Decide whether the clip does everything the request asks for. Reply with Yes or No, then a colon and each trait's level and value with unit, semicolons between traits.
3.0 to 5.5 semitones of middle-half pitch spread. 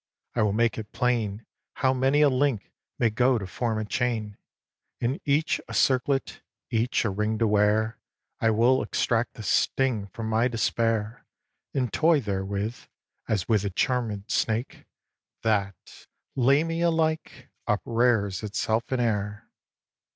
Yes: average, 3.3 semitones